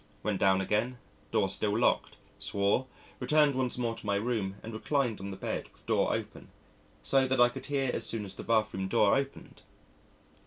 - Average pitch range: Yes, average, 4.3 semitones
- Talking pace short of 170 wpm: No, average, 195 wpm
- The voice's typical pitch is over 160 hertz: No, low, 115 Hz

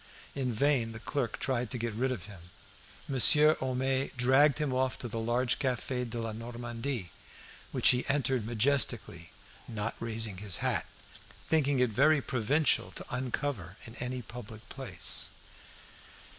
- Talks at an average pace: Yes, average, 145 wpm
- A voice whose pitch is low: Yes, low, 125 Hz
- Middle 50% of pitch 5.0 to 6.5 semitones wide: No, average, 2.9 semitones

